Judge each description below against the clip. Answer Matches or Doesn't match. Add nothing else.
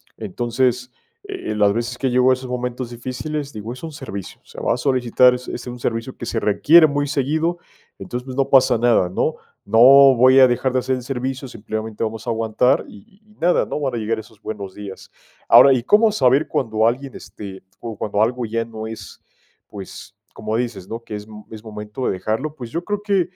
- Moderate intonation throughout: Matches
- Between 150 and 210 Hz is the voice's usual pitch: Doesn't match